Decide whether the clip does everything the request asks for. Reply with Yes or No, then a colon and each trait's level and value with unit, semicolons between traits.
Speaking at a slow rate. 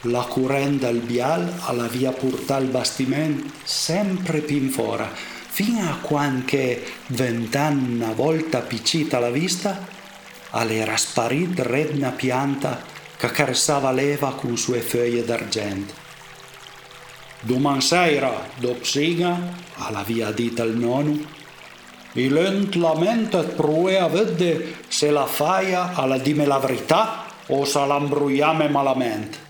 Yes: slow, 110 wpm